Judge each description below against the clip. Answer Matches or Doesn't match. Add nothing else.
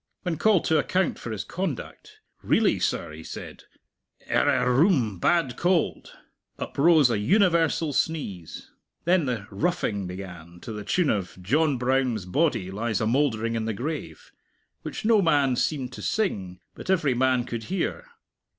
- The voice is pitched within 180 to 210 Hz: Doesn't match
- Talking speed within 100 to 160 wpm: Matches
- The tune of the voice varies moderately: Doesn't match